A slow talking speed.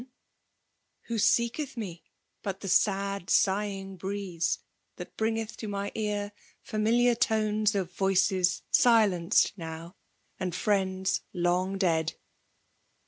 Yes: slow, 110 wpm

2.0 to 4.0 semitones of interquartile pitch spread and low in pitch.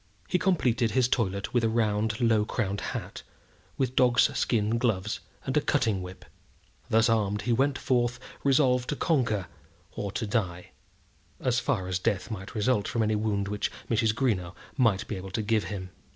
Yes: average, 3.3 semitones; low, 110 Hz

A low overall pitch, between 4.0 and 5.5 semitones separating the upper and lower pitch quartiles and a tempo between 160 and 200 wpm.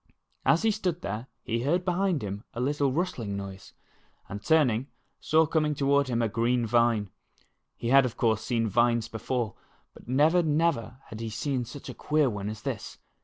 Yes: low, 125 Hz; average, 5.1 semitones; average, 180 wpm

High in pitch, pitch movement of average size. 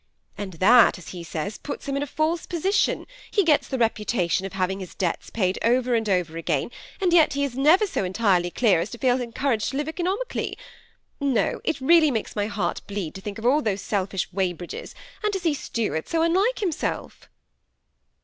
No: high, 230 Hz; wide, 7.9 semitones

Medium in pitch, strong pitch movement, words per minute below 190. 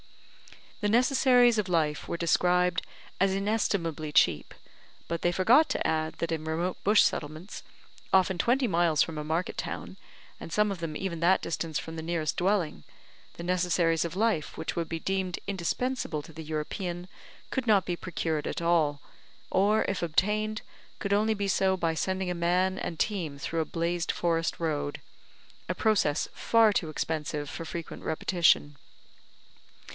No: medium, 175 Hz; average, 3.5 semitones; average, 160 wpm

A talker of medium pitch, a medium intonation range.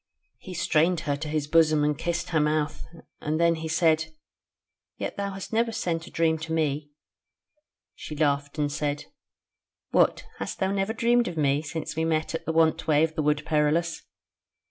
No: medium, 160 Hz; narrow, 2.0 semitones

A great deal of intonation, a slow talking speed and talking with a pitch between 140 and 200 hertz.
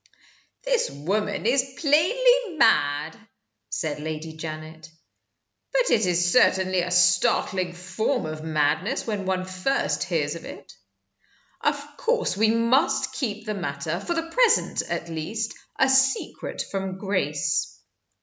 Yes: wide, 8.6 semitones; slow, 130 wpm; high, 190 Hz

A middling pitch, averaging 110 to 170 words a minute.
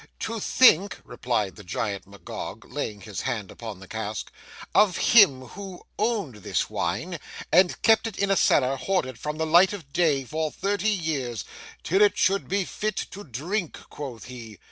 Yes: medium, 155 Hz; average, 165 wpm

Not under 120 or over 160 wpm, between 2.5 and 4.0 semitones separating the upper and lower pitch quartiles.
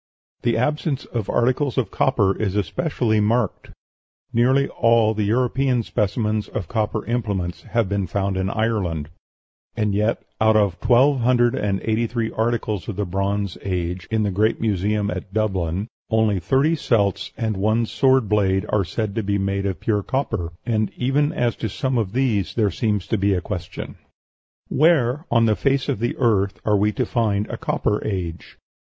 No: average, 175 wpm; average, 3.2 semitones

